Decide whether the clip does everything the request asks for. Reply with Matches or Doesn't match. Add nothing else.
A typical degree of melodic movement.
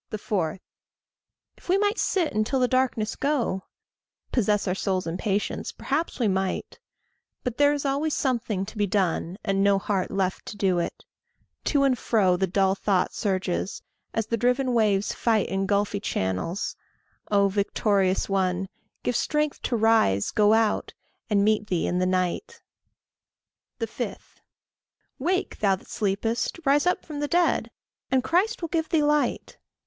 Doesn't match